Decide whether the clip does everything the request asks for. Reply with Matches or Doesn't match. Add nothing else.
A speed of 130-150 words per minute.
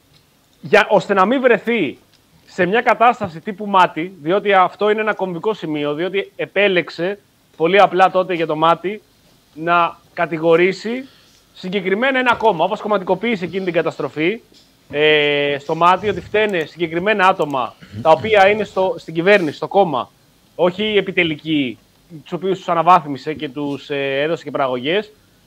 Matches